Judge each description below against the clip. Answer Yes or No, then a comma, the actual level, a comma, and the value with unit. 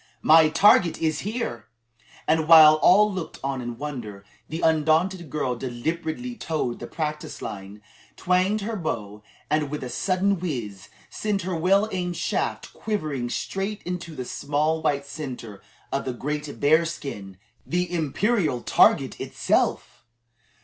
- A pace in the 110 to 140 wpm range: Yes, slow, 135 wpm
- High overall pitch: No, medium, 155 Hz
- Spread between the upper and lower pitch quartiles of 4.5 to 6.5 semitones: Yes, average, 5.3 semitones